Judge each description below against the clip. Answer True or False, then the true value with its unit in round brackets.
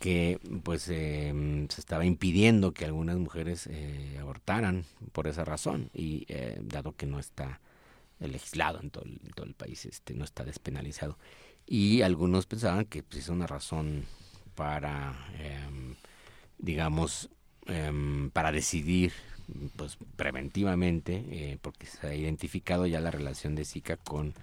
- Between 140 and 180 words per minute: True (145 wpm)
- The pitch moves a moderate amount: True (3.4 semitones)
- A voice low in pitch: True (80 Hz)